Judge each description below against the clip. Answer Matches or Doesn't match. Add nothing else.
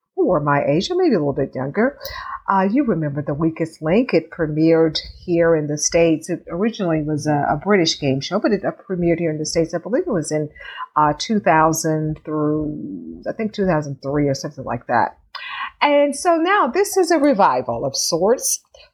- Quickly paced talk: Doesn't match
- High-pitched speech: Doesn't match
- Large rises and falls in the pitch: Matches